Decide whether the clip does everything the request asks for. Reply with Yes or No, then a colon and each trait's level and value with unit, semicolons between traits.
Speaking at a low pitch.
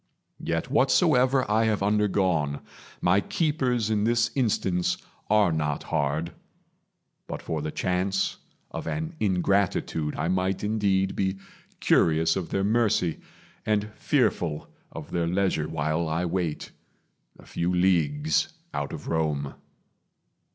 Yes: very low, 95 Hz